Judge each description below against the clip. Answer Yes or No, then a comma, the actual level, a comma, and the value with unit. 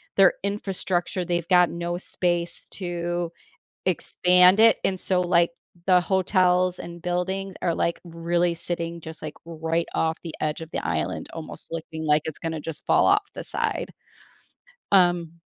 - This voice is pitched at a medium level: Yes, medium, 175 Hz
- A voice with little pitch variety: Yes, narrow, 1.6 semitones